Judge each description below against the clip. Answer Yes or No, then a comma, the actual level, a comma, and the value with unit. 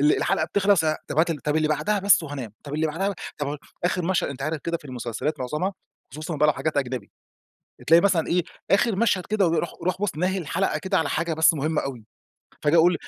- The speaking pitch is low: No, medium, 160 Hz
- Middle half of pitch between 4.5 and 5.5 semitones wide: No, average, 3.6 semitones